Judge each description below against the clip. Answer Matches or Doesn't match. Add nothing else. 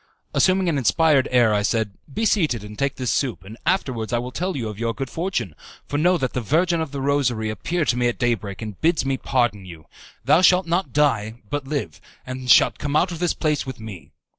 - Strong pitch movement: Matches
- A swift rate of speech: Matches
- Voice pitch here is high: Doesn't match